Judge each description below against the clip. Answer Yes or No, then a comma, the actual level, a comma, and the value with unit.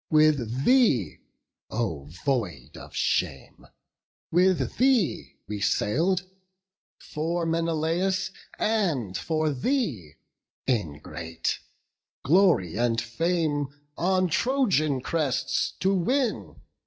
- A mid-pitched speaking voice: Yes, medium, 155 Hz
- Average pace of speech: No, slow, 85 wpm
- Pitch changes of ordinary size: No, wide, 8.2 semitones